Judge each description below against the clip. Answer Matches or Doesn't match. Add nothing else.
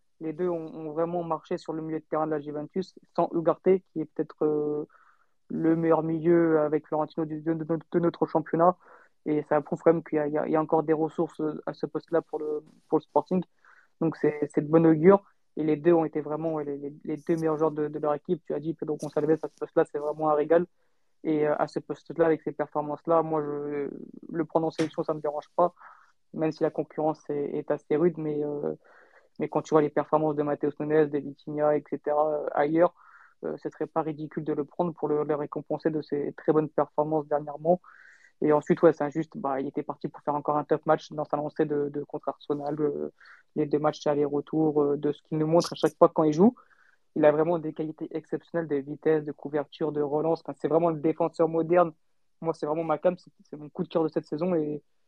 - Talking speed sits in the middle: Doesn't match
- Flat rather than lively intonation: Matches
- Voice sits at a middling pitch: Matches